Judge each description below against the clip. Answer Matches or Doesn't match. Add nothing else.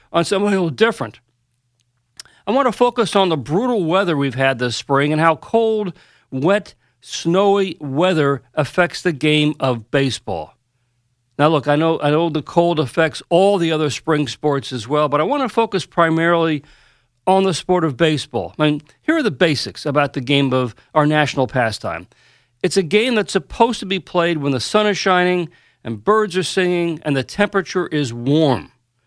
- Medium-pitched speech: Matches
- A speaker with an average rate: Matches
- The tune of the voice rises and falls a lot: Matches